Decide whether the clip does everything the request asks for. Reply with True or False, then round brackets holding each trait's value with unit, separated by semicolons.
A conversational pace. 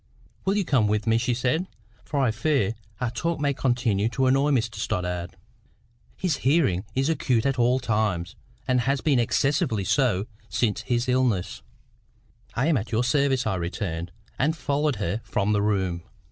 True (170 wpm)